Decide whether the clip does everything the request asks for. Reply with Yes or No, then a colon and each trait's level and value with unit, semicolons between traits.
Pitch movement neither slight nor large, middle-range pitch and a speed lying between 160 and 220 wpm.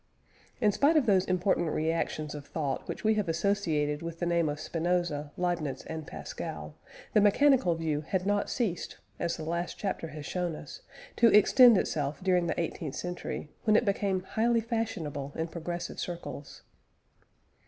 Yes: average, 4.5 semitones; medium, 175 Hz; average, 165 wpm